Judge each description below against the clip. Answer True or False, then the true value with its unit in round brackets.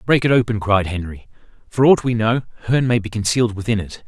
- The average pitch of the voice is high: False (110 Hz)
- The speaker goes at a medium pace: False (220 wpm)